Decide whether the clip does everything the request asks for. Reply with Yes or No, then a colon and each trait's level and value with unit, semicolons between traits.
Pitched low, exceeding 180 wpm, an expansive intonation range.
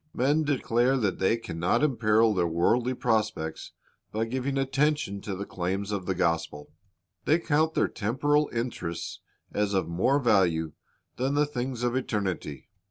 No: low, 115 Hz; average, 155 wpm; wide, 6.0 semitones